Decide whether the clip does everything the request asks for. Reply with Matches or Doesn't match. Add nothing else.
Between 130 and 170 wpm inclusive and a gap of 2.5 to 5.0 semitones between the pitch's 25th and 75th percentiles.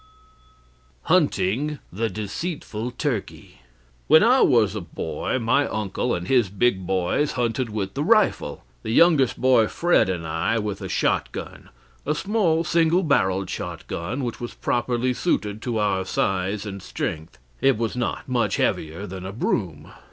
Doesn't match